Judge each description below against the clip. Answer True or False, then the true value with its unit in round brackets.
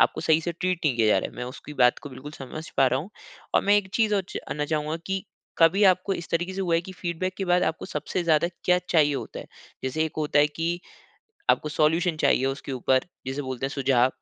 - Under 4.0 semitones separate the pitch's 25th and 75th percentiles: False (4.6 semitones)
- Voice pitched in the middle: True (160 Hz)